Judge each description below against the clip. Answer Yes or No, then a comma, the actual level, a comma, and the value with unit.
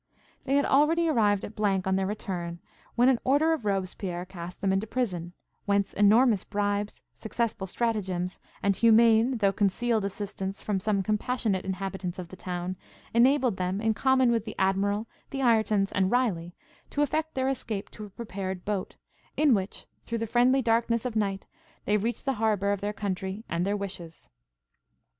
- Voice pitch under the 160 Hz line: No, high, 205 Hz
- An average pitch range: Yes, average, 3.5 semitones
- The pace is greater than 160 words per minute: Yes, average, 170 wpm